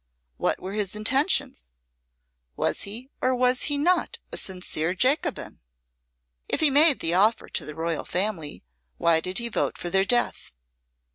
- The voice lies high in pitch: Yes, high, 215 Hz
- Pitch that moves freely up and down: Yes, wide, 6.7 semitones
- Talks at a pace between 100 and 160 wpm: Yes, average, 155 wpm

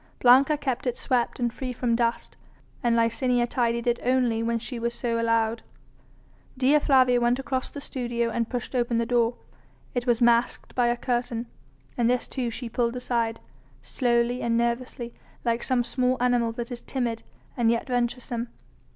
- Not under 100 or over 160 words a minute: No, average, 170 wpm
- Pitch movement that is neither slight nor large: No, narrow, 1.2 semitones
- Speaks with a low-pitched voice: No, high, 240 Hz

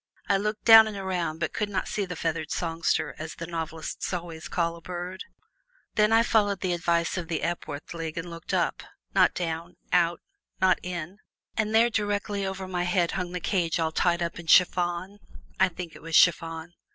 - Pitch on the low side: No, medium, 175 Hz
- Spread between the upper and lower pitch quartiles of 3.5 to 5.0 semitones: No, narrow, 2.5 semitones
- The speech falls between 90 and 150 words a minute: No, average, 195 wpm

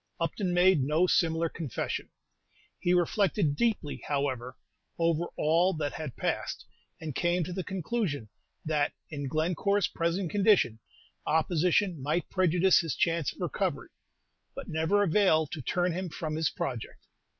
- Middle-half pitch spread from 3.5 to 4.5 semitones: No, average, 3.1 semitones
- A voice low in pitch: No, medium, 165 Hz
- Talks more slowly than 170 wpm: Yes, average, 140 wpm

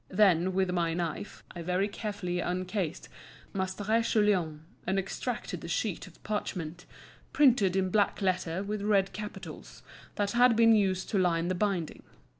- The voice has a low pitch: No, high, 190 Hz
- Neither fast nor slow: Yes, average, 150 wpm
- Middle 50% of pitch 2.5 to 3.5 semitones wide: Yes, average, 2.8 semitones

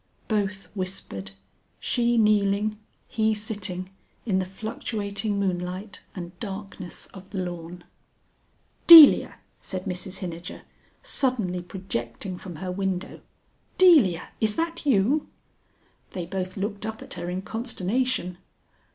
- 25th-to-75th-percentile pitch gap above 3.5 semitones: No, average, 3.1 semitones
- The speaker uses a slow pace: Yes, slow, 115 wpm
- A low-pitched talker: No, high, 195 Hz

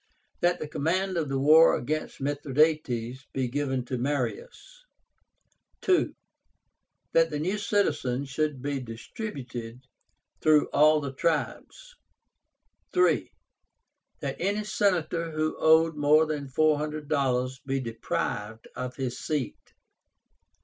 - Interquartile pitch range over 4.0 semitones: No, average, 3.7 semitones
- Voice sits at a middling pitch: Yes, medium, 150 Hz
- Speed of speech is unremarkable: No, slow, 115 wpm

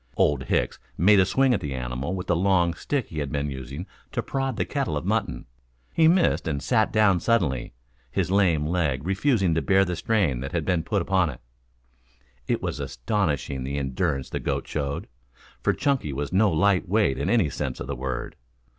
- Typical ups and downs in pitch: No, wide, 6.4 semitones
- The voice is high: No, very low, 85 Hz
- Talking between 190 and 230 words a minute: Yes, average, 200 wpm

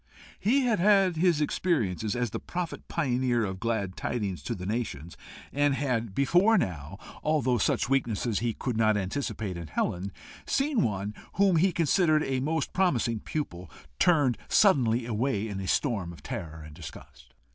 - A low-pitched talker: Yes, low, 120 Hz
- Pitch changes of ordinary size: No, wide, 7.9 semitones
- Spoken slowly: No, average, 160 wpm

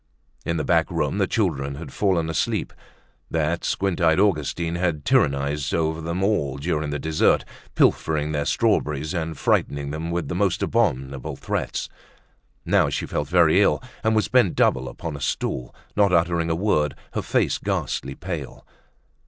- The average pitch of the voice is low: Yes, very low, 80 Hz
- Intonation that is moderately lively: Yes, average, 3.1 semitones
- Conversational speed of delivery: Yes, average, 160 wpm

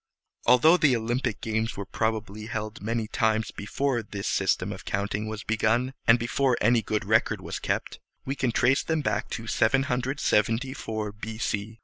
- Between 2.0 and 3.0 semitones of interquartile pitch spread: Yes, average, 2.7 semitones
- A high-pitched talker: No, low, 115 Hz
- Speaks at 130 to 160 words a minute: Yes, average, 155 wpm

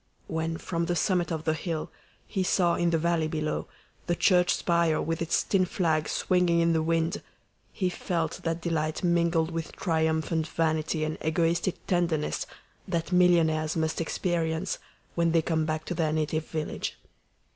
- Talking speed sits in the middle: Yes, average, 160 wpm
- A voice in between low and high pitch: Yes, medium, 165 Hz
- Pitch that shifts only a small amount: Yes, narrow, 1.5 semitones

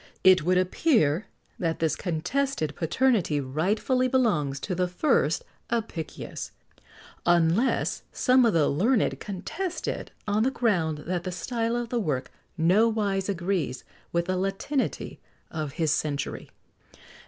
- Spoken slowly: Yes, slow, 130 wpm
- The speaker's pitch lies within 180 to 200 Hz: Yes, medium, 185 Hz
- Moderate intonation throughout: No, wide, 6.2 semitones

